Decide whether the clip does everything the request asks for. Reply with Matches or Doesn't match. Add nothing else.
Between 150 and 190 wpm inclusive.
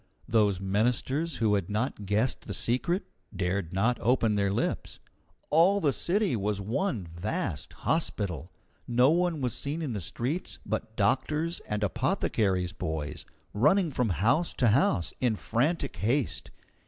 Doesn't match